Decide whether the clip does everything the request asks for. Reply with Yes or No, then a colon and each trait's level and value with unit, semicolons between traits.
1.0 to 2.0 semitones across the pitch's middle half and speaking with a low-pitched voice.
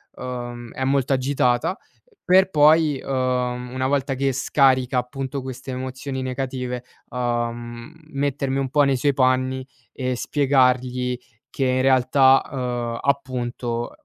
Yes: narrow, 1.6 semitones; low, 130 Hz